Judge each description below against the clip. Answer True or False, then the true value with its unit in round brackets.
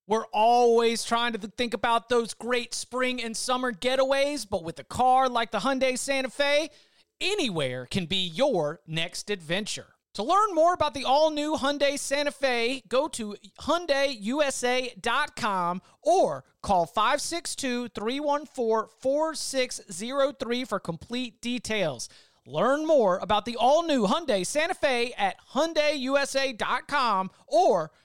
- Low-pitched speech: False (250 Hz)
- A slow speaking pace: True (120 wpm)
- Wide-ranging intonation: False (4.1 semitones)